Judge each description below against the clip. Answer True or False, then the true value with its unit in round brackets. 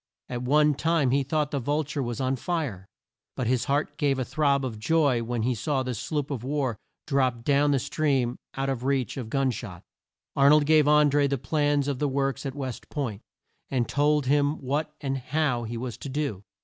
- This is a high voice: False (135 Hz)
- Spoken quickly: True (215 wpm)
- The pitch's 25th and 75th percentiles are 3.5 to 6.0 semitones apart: False (2.7 semitones)